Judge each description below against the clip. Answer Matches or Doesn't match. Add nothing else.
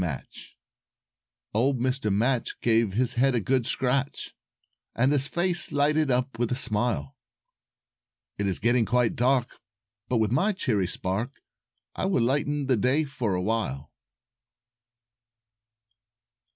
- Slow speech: Matches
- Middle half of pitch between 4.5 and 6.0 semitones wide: Doesn't match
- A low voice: Matches